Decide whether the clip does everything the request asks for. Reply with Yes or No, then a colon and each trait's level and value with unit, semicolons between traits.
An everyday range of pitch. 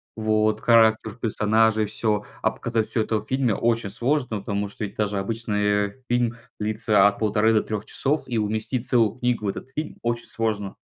No: narrow, 2.0 semitones